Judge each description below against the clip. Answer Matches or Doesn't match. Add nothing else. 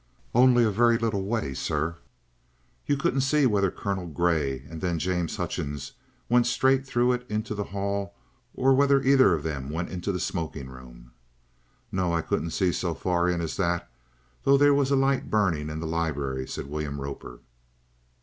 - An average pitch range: Doesn't match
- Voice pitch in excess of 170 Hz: Doesn't match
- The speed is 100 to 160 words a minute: Doesn't match